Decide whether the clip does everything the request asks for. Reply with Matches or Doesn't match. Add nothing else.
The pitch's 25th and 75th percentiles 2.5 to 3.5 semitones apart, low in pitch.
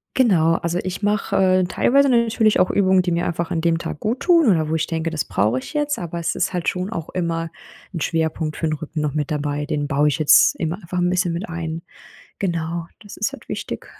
Doesn't match